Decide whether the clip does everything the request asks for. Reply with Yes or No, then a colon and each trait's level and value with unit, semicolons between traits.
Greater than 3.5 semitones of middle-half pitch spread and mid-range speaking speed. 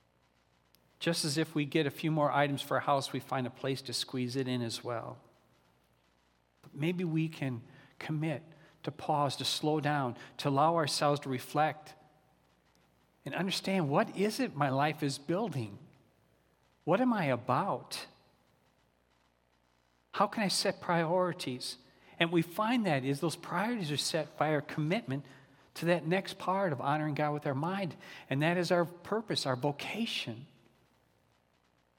Yes: average, 4.3 semitones; average, 160 wpm